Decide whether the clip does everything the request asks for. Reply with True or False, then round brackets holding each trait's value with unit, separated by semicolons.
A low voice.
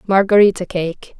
False (190 Hz)